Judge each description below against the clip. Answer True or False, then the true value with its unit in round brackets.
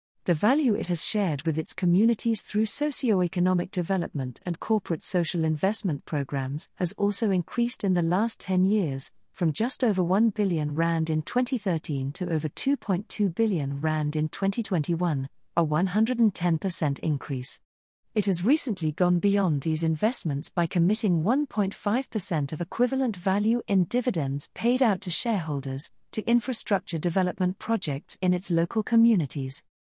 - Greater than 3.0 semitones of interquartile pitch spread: True (5.5 semitones)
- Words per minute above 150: False (140 wpm)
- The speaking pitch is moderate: True (180 Hz)